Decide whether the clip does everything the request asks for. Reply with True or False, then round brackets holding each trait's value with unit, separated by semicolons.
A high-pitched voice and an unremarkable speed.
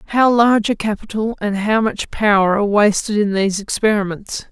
True (210 Hz; 175 wpm)